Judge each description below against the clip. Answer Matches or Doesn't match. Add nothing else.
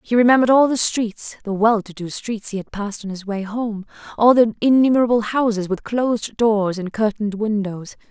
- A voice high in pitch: Matches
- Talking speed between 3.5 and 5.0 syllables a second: Doesn't match